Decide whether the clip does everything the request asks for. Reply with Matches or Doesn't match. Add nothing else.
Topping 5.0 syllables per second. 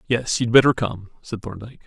Matches